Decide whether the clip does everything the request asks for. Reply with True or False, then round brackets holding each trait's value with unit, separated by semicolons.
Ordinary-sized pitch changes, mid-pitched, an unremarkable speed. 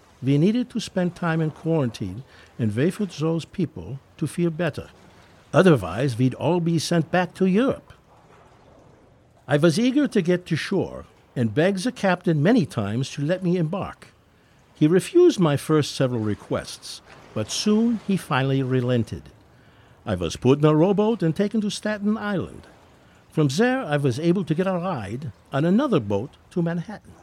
False (6.6 semitones; 155 Hz; 170 wpm)